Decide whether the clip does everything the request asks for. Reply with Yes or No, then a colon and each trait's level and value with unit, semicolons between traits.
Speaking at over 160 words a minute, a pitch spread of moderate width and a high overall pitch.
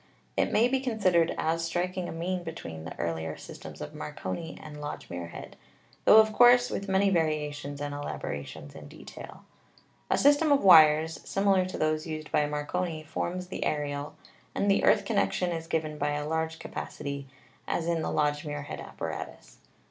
No: average, 170 wpm; average, 4.0 semitones; medium, 160 Hz